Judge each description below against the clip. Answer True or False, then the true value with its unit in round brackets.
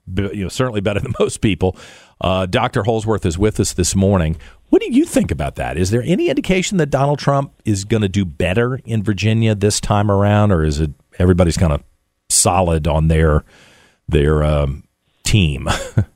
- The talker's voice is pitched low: True (100 Hz)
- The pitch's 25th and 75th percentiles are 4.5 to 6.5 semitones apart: True (5.5 semitones)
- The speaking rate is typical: True (185 wpm)